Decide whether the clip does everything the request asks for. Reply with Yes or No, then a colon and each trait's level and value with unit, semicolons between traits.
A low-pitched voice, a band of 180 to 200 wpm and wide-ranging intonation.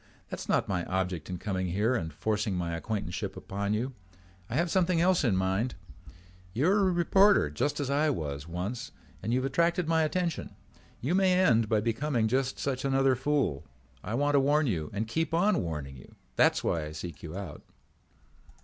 Yes: low, 120 Hz; average, 195 wpm; wide, 8.4 semitones